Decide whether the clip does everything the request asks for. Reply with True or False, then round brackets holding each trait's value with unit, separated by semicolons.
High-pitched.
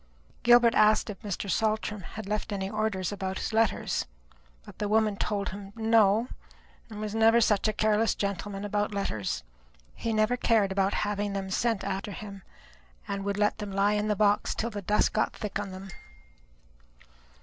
True (210 Hz)